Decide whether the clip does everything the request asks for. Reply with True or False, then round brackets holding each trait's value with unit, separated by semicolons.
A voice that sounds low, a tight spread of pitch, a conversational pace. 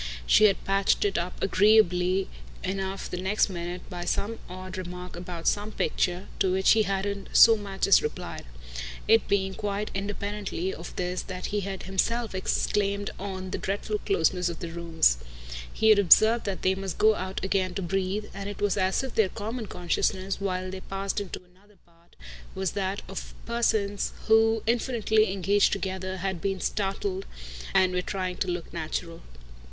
False (195 Hz; 2.0 semitones; 170 wpm)